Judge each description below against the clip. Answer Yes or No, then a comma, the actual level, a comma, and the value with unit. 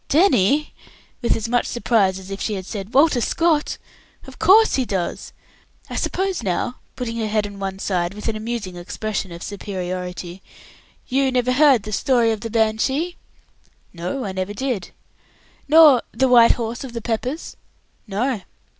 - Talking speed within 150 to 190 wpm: Yes, average, 160 wpm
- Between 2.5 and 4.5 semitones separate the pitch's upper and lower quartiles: No, average, 4.9 semitones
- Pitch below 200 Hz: No, high, 225 Hz